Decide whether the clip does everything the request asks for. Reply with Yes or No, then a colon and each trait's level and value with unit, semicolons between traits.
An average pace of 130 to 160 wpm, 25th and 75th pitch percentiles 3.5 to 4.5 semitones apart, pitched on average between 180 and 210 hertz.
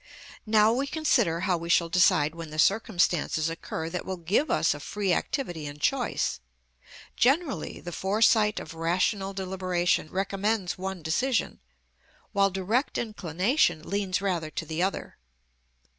Yes: average, 140 wpm; average, 4.1 semitones; high, 190 Hz